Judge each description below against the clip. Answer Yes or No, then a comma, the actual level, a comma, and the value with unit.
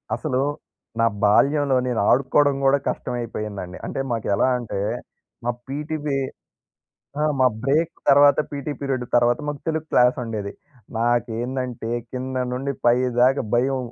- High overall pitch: No, low, 130 Hz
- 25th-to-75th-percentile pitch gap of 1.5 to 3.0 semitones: Yes, average, 2.7 semitones